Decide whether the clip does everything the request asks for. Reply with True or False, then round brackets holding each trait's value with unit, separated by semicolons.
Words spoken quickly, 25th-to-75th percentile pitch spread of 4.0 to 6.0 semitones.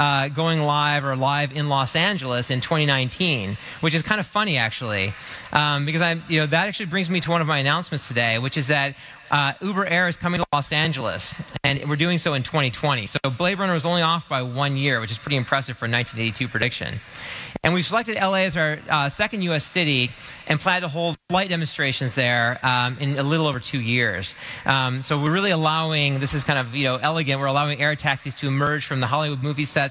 False (225 wpm; 3.6 semitones)